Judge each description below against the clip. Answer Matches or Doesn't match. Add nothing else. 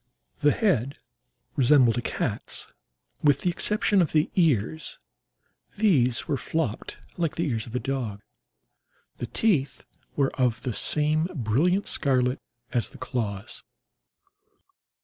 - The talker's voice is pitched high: Doesn't match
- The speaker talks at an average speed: Doesn't match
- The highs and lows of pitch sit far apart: Doesn't match